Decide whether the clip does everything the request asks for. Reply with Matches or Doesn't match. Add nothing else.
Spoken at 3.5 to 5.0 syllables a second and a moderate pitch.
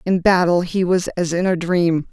Matches